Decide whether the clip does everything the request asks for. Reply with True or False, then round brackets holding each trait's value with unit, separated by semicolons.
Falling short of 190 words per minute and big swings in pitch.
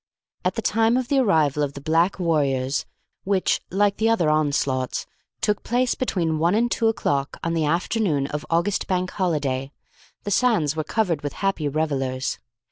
True (170 wpm; 6.0 semitones)